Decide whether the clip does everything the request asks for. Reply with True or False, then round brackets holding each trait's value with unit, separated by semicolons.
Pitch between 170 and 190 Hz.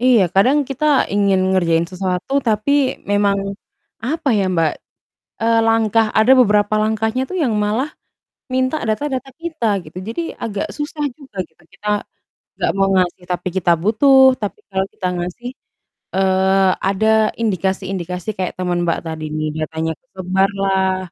False (205 Hz)